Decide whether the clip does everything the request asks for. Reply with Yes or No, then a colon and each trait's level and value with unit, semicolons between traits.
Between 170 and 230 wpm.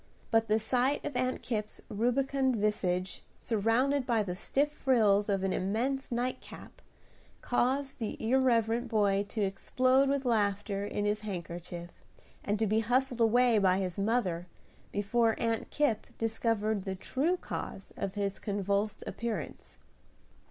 No: average, 140 wpm